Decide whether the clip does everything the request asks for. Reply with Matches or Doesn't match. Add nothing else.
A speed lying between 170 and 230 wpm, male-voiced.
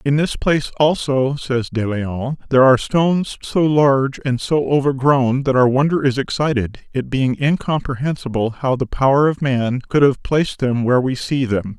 Matches